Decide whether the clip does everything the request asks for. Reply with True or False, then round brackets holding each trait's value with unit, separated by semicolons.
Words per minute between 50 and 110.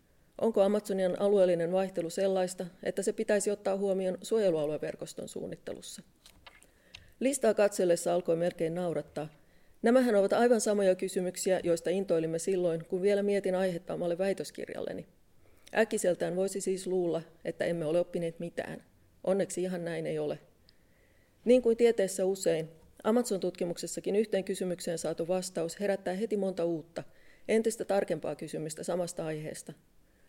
False (125 wpm)